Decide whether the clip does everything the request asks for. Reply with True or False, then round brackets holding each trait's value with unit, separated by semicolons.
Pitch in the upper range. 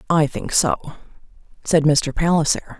False (155 Hz)